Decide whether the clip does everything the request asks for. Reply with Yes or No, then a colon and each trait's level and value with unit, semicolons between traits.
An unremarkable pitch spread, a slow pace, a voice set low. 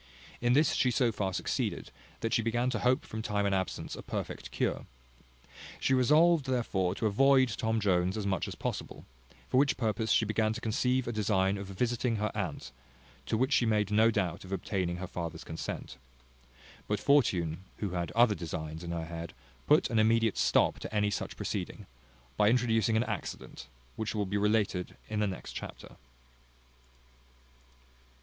No: average, 4.0 semitones; average, 175 wpm; low, 110 Hz